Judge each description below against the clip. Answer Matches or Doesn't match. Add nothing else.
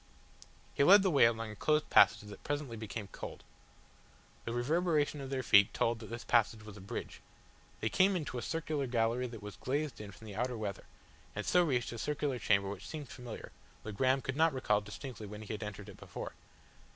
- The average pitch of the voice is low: Matches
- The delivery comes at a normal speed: Doesn't match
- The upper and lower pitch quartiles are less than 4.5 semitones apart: Doesn't match